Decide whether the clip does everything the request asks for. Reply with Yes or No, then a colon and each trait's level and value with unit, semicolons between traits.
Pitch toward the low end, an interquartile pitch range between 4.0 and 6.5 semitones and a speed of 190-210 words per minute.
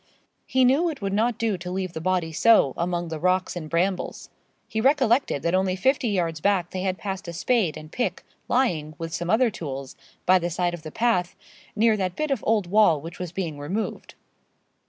No: medium, 185 Hz; average, 4.7 semitones; fast, 205 wpm